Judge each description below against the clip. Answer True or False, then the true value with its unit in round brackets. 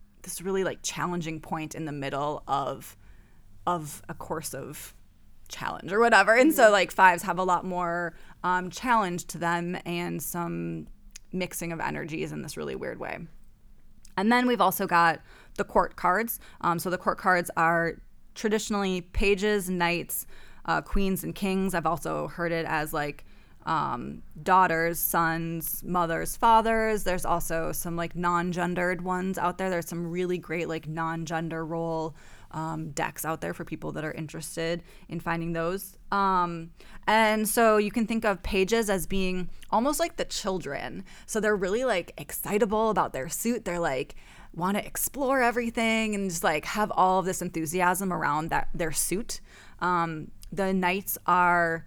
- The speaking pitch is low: False (175 Hz)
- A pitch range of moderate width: True (3.0 semitones)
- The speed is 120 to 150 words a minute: False (165 wpm)